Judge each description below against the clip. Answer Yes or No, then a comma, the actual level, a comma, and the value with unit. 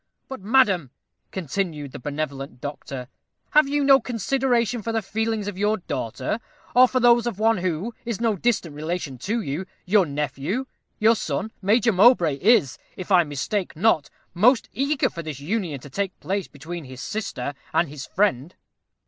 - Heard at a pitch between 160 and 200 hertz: Yes, high, 190 Hz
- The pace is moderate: Yes, average, 165 wpm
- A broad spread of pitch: Yes, wide, 7.3 semitones